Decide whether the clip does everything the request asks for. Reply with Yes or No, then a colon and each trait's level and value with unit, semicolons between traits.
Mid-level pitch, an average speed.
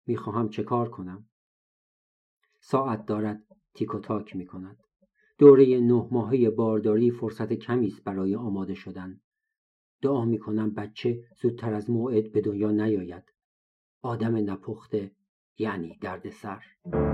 No: low, 110 Hz; average, 125 wpm